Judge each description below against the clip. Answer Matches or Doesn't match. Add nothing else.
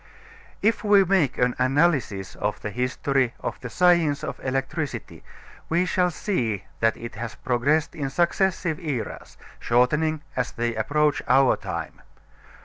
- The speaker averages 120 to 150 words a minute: Matches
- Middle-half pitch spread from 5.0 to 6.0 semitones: Matches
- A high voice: Doesn't match